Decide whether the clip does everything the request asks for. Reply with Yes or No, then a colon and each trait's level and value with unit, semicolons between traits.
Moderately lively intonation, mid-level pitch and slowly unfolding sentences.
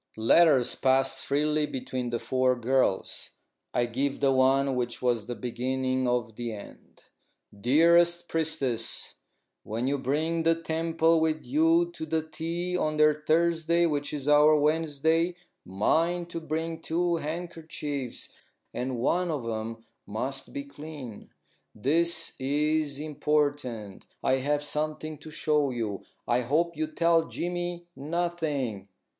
Yes: average, 4.2 semitones; medium, 150 Hz; slow, 130 wpm